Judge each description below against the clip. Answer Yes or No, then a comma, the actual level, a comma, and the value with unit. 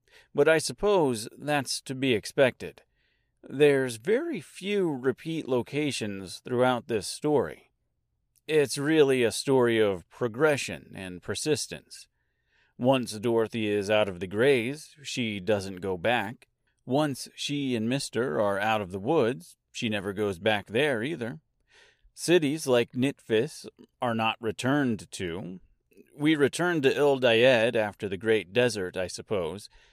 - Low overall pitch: Yes, low, 125 Hz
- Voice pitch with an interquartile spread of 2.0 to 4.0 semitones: No, average, 4.9 semitones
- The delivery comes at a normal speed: No, slow, 130 wpm